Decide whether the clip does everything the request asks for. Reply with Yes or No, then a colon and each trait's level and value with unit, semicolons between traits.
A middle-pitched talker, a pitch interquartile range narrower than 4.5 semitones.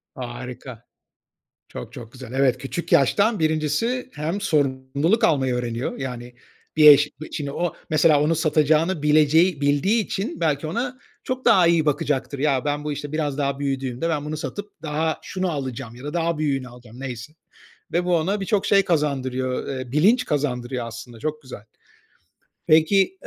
Yes: medium, 150 Hz; average, 4.0 semitones